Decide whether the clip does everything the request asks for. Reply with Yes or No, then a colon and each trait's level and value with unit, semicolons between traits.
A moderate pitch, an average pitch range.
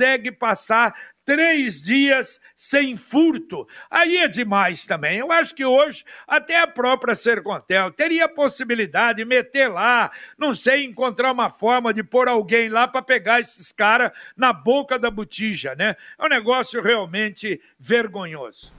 No: high, 245 Hz; average, 3.5 semitones